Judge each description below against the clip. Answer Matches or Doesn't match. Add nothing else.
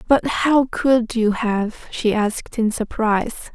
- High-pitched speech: Matches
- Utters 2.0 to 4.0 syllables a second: Matches